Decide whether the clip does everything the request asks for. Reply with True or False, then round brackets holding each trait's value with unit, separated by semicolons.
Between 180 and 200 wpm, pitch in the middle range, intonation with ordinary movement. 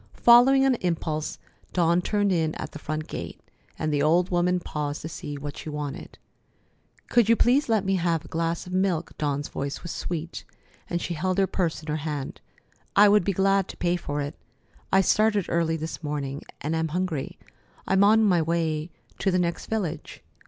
True (190 wpm; 170 Hz; 3.8 semitones)